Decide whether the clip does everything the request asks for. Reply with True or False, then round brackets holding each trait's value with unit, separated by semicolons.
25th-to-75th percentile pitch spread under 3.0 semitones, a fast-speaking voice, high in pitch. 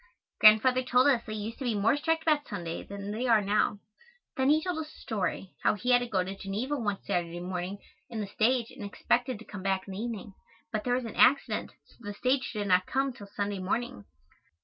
False (4.1 semitones; 230 wpm; 215 Hz)